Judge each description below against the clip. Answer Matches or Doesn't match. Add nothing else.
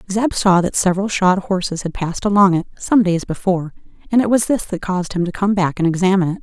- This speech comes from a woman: Matches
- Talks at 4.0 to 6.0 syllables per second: Doesn't match